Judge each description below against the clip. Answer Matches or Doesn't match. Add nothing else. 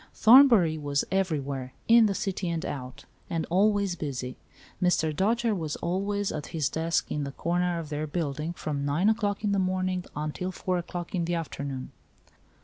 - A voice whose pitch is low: Doesn't match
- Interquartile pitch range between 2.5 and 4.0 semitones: Doesn't match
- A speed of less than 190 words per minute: Matches